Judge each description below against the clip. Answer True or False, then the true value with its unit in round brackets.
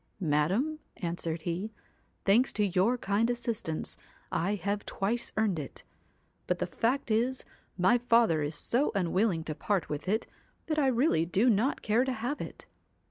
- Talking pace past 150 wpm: True (160 wpm)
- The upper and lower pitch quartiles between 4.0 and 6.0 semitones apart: True (5.6 semitones)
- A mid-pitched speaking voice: False (205 Hz)